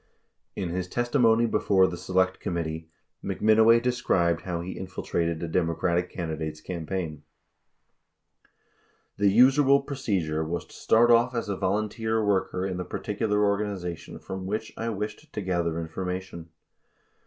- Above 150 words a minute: No, average, 140 wpm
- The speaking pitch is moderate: No, very low, 95 Hz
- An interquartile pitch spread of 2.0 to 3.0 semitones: No, average, 4.3 semitones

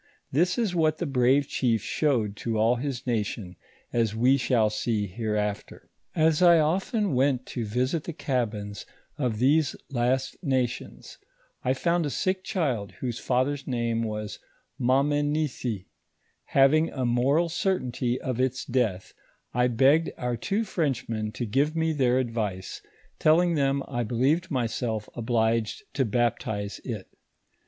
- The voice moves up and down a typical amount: Yes, average, 4.3 semitones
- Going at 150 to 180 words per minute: No, average, 140 wpm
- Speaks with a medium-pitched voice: No, low, 125 Hz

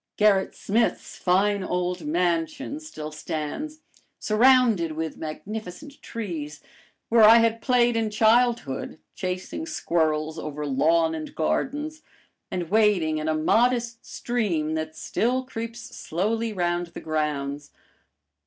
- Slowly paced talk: Yes, slow, 115 wpm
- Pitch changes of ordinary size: No, wide, 6.6 semitones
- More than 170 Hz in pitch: Yes, medium, 185 Hz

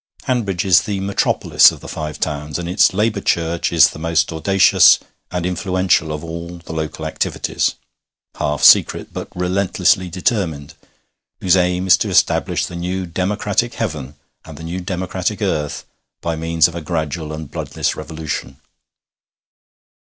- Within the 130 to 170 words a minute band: Yes, average, 150 wpm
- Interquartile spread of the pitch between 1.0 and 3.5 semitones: Yes, average, 2.8 semitones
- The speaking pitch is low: Yes, very low, 85 Hz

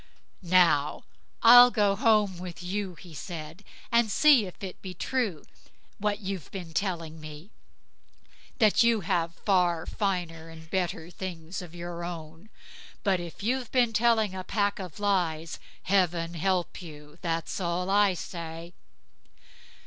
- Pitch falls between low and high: Yes, medium, 180 Hz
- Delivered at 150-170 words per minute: No, average, 140 wpm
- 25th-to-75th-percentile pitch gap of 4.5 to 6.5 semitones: No, average, 3.5 semitones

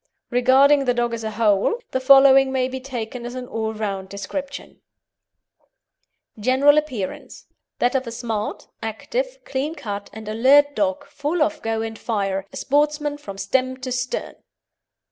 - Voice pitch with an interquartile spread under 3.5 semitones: No, average, 4.1 semitones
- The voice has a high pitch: Yes, very high, 255 Hz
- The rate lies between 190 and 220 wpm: No, average, 155 wpm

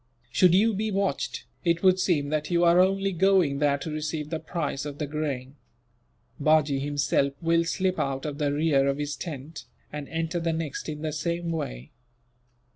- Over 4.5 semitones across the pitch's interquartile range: No, average, 3.0 semitones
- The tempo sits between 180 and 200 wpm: Yes, average, 185 wpm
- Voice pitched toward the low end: No, medium, 155 Hz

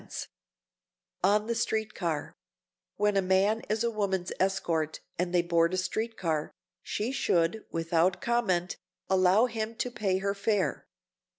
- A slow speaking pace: No, average, 150 wpm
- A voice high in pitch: Yes, high, 195 Hz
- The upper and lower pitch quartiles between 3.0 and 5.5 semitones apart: Yes, average, 3.7 semitones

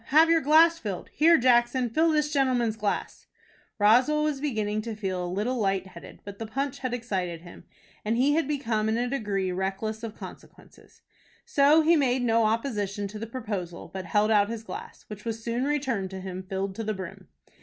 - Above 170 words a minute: Yes, average, 195 wpm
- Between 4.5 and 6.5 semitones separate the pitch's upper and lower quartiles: Yes, average, 4.9 semitones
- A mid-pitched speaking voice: No, high, 225 Hz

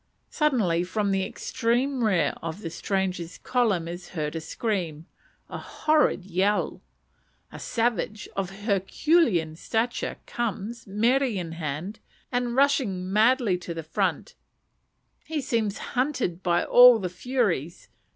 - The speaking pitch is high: Yes, high, 205 Hz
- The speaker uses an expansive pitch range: Yes, wide, 5.7 semitones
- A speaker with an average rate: No, slow, 125 wpm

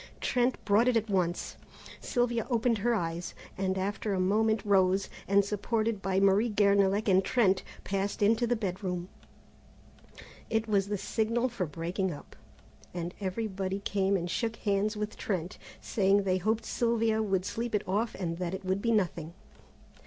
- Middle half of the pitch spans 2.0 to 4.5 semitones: Yes, average, 2.8 semitones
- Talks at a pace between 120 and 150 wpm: No, average, 160 wpm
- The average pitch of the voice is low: No, high, 200 Hz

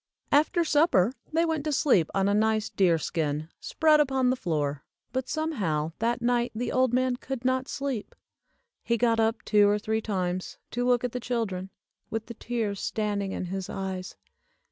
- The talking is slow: No, average, 185 wpm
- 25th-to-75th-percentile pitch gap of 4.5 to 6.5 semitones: Yes, average, 5.1 semitones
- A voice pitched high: Yes, high, 225 Hz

